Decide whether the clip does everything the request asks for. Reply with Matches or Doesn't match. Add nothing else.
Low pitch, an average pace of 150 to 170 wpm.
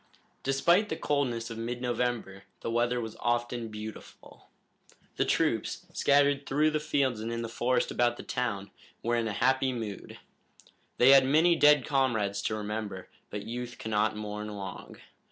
Matches